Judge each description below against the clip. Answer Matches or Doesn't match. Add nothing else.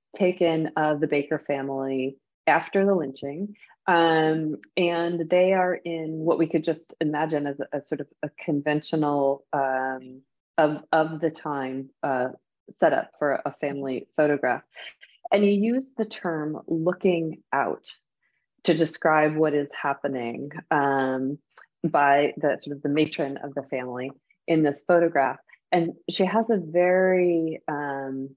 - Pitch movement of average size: Matches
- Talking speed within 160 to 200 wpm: Doesn't match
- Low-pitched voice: Doesn't match